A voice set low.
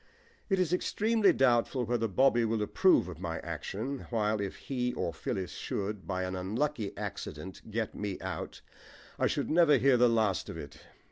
Yes: low, 110 Hz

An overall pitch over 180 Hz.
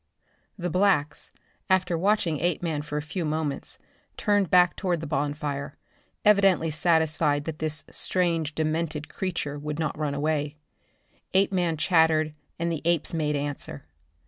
No: medium, 160 Hz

